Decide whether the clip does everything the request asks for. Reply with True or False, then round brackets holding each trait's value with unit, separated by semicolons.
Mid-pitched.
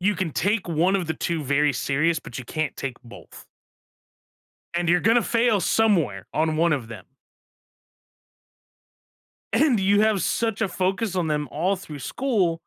True (175 Hz)